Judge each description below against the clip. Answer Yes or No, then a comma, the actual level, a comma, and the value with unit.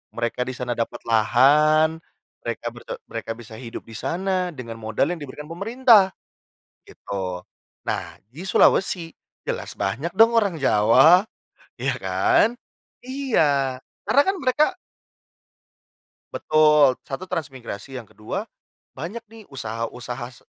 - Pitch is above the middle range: No, medium, 140 Hz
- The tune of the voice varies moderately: No, wide, 7.7 semitones